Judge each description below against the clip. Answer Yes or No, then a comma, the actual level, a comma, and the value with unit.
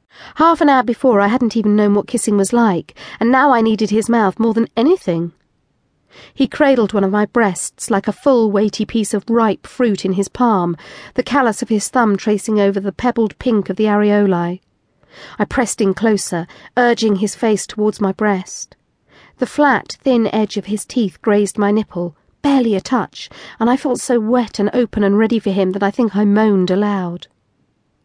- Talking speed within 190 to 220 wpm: Yes, average, 195 wpm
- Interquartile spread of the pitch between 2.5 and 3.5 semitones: Yes, average, 3.2 semitones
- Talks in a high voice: Yes, high, 215 Hz